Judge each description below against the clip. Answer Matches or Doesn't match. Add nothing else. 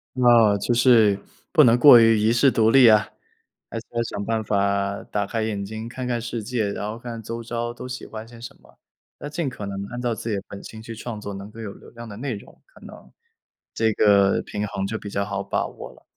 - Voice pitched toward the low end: Matches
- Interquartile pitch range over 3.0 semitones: Doesn't match